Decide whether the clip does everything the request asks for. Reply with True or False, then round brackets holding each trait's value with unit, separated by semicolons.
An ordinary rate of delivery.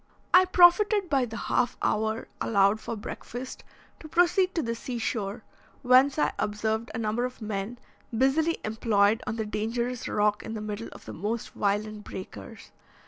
True (165 wpm)